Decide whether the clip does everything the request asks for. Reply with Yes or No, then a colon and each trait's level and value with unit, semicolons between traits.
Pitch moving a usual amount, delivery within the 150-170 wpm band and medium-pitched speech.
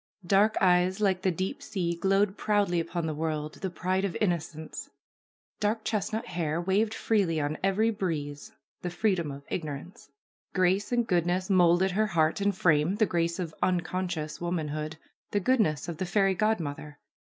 Yes: average, 3.6 semitones; average, 160 wpm; medium, 180 Hz